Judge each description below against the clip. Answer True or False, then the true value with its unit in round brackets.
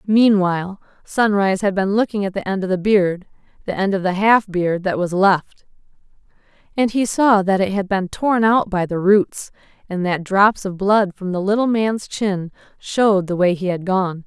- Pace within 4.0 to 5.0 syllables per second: True (4.7 syllables/s)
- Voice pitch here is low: False (195 Hz)